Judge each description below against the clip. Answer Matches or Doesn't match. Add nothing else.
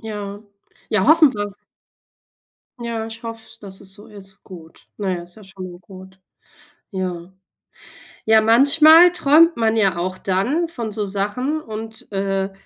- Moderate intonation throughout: Matches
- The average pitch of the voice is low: Doesn't match